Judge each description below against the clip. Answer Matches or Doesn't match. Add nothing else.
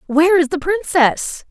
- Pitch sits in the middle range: Doesn't match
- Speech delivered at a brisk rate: Doesn't match